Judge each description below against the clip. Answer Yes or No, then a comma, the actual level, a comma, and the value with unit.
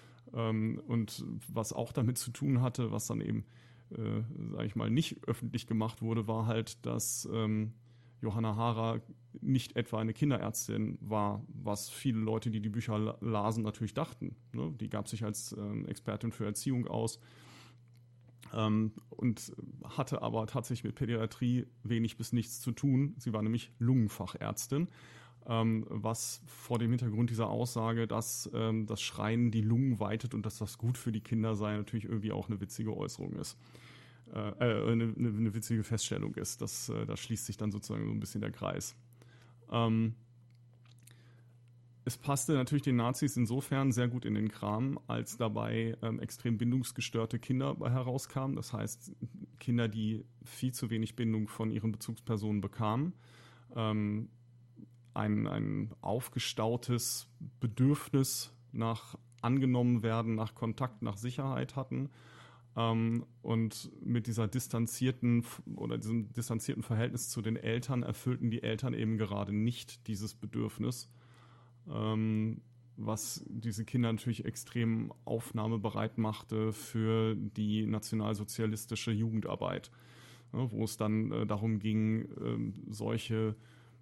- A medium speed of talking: Yes, average, 135 wpm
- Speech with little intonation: Yes, narrow, 1.8 semitones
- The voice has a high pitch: No, low, 115 Hz